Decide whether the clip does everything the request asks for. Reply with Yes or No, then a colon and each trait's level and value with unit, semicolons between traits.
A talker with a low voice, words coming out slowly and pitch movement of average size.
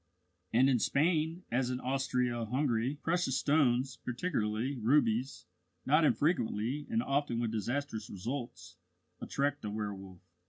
Yes: low, 125 Hz; slow, 120 wpm; average, 3.9 semitones